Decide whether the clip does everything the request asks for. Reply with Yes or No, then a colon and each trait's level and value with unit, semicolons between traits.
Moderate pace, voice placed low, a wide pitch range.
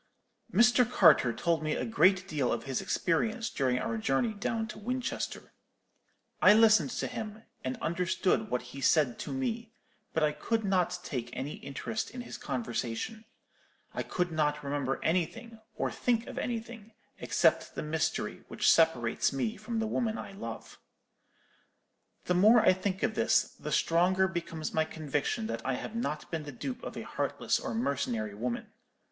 No: average, 165 wpm; medium, 180 Hz; wide, 8.0 semitones